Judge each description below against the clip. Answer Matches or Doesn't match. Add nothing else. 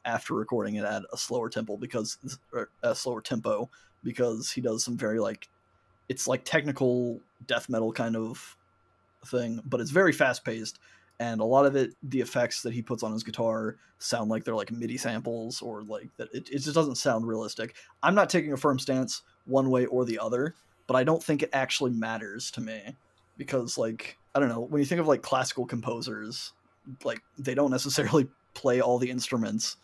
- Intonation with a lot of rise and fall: Doesn't match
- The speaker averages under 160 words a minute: Doesn't match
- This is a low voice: Matches